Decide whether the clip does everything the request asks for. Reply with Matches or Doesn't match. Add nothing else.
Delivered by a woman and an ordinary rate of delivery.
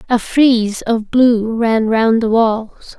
Matches